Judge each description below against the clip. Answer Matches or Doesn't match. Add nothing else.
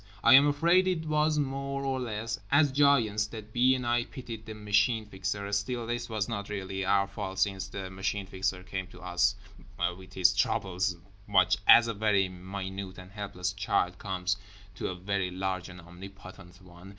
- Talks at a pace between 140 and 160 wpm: Doesn't match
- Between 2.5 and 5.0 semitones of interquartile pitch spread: Matches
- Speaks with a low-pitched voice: Matches